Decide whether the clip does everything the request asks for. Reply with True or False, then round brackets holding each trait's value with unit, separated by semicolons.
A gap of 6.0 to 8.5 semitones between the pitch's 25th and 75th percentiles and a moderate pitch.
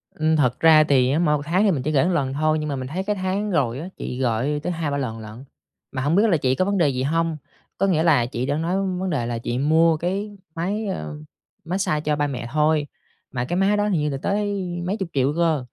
False (5.2 semitones; 155 Hz)